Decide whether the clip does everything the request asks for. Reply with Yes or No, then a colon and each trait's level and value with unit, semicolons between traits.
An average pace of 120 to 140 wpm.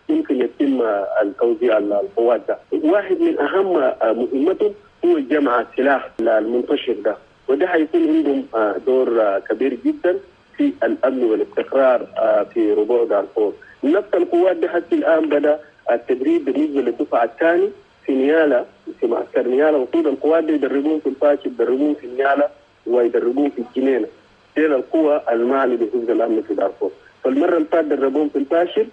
Yes: slow, 135 wpm